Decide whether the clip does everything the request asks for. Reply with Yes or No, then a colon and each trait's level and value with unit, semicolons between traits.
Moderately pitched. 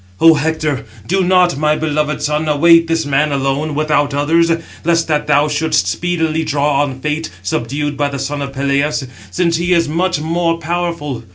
Yes: medium, 150 Hz